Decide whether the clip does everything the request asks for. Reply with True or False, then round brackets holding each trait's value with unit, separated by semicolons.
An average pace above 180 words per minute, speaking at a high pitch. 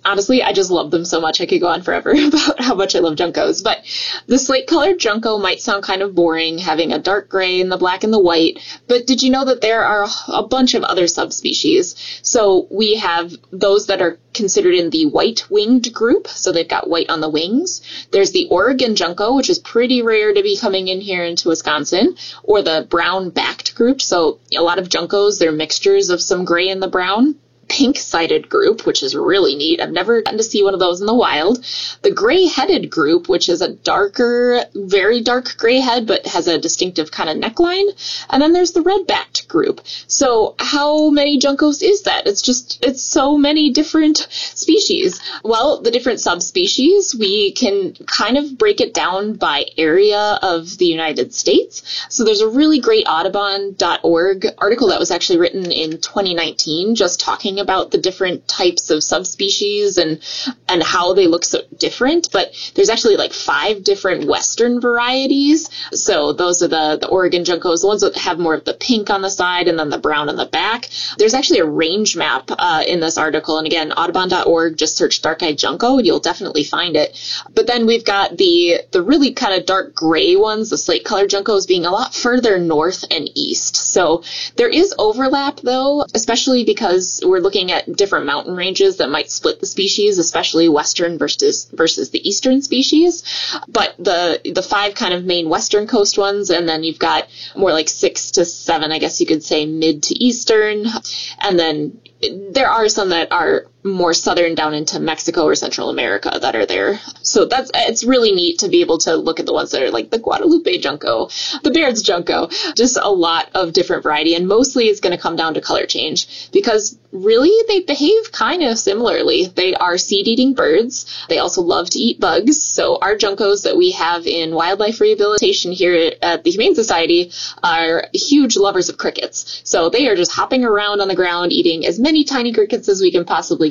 True (200 wpm; 240 Hz)